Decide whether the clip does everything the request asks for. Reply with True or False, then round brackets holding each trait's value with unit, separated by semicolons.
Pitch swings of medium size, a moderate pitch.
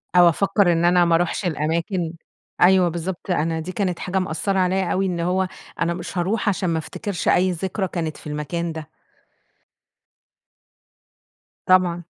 False (2.1 semitones; 175 Hz)